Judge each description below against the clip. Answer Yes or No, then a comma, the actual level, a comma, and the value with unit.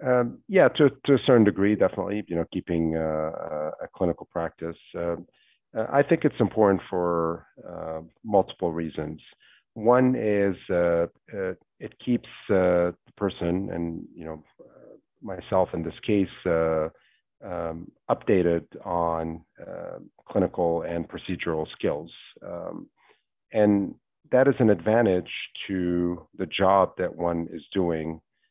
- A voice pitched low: Yes, very low, 90 Hz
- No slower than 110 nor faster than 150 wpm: Yes, slow, 135 wpm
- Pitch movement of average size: Yes, average, 4.2 semitones